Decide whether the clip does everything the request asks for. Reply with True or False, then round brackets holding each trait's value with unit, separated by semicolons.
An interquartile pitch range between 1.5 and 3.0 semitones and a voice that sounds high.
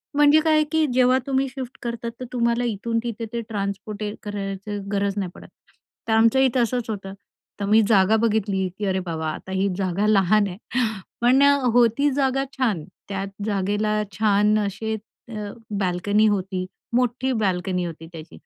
False (3.5 semitones; 210 Hz)